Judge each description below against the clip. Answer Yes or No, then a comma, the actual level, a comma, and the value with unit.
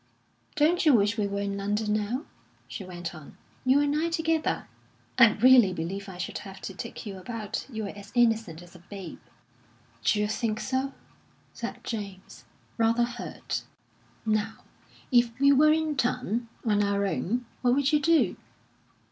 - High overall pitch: Yes, high, 220 Hz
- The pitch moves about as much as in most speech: Yes, average, 4.5 semitones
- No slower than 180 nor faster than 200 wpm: No, average, 160 wpm